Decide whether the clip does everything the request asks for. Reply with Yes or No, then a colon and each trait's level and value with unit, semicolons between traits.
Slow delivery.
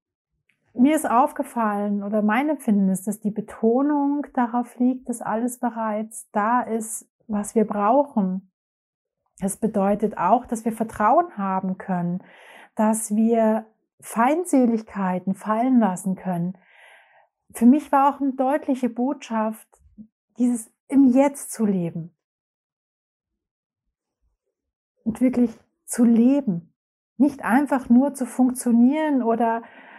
Yes: slow, 110 wpm